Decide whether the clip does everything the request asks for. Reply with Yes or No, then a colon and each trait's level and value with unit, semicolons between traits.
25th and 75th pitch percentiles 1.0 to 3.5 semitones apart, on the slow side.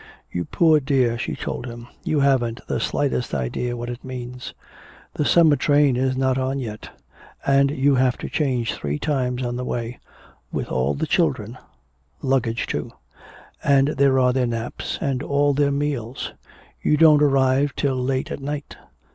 No: narrow, 2.5 semitones; average, 165 wpm